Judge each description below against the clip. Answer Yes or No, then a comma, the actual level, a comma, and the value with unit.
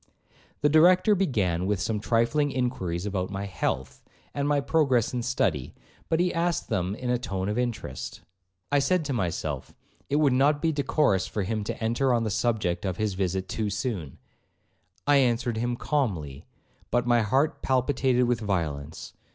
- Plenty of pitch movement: Yes, wide, 6.5 semitones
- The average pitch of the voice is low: Yes, low, 120 Hz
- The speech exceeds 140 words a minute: Yes, average, 170 wpm